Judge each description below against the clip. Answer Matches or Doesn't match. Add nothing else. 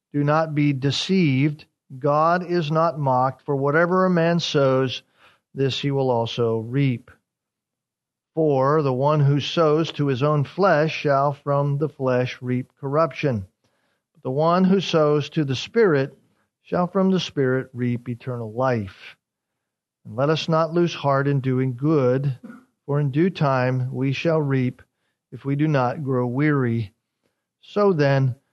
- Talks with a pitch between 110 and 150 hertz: Matches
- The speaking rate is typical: Matches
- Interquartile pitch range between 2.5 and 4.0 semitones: Matches